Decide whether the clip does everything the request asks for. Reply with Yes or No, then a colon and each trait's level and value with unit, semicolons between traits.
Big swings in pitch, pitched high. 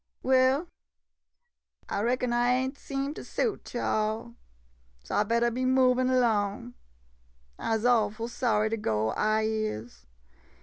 No: average, 3.1 semitones; high, 235 Hz